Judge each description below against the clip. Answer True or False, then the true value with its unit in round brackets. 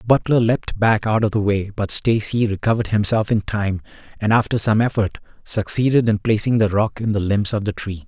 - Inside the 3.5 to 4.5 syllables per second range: False (5.5 syllables/s)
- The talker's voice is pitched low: True (105 Hz)